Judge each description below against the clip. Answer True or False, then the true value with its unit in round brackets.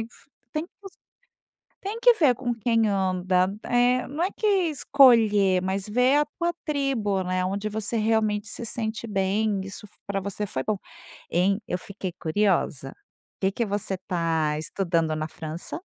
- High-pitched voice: True (205 Hz)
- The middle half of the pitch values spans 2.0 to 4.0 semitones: False (4.4 semitones)